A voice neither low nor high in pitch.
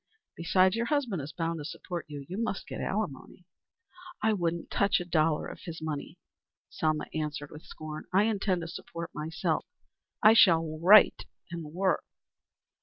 Yes: medium, 170 Hz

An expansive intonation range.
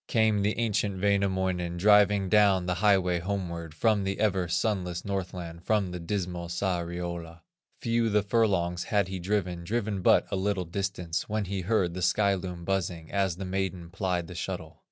No: average, 2.7 semitones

